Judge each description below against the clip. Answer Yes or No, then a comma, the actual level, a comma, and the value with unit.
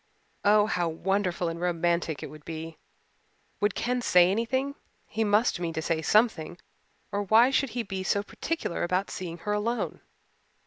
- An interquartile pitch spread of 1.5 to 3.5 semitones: No, average, 4.4 semitones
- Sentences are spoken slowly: No, average, 165 wpm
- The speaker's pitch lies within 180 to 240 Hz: Yes, high, 190 Hz